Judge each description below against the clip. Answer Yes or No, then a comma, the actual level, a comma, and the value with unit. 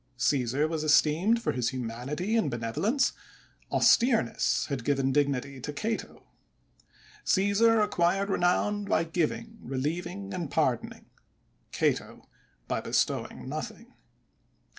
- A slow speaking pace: Yes, slow, 110 wpm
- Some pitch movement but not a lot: No, wide, 6.9 semitones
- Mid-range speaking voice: Yes, medium, 160 Hz